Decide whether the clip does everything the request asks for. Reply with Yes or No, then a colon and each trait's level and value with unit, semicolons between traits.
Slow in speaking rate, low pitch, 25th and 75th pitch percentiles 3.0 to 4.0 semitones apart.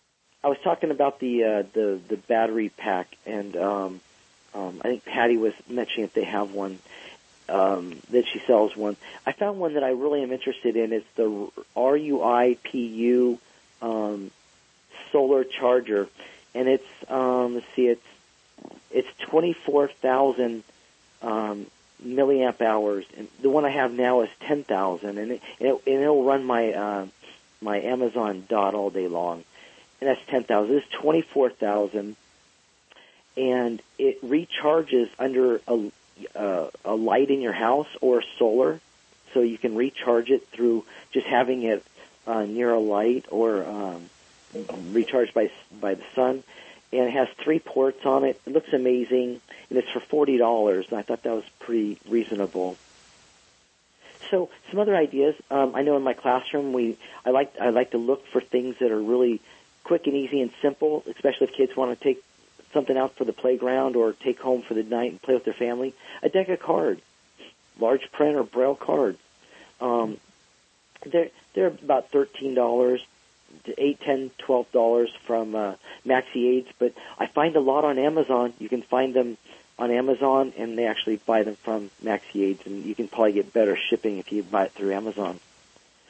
No: average, 175 wpm; low, 120 Hz; average, 3.7 semitones